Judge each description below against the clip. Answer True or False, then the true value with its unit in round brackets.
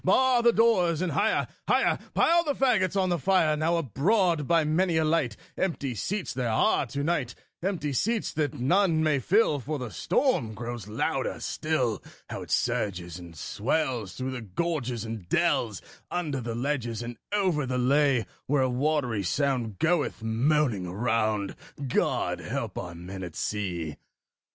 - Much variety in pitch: True (6.9 semitones)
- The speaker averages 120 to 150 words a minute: False (160 wpm)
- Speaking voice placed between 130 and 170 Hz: True (140 Hz)